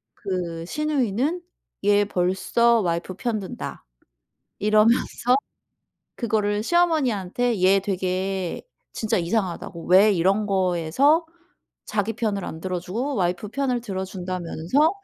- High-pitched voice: Yes, high, 200 Hz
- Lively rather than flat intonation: No, average, 4.4 semitones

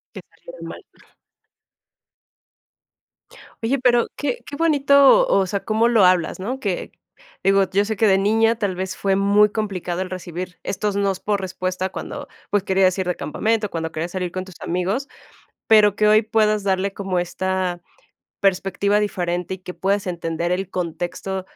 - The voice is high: Yes, high, 195 Hz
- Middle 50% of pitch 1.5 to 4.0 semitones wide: Yes, narrow, 2.6 semitones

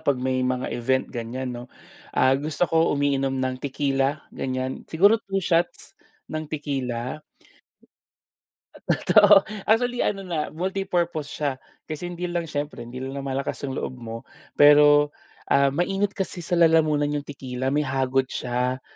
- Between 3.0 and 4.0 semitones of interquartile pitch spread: No, average, 4.5 semitones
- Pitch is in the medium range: Yes, medium, 145 Hz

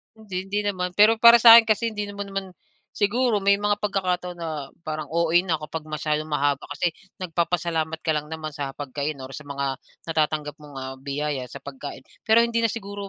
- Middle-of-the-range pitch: Yes, medium, 170 Hz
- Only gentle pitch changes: No, average, 5.2 semitones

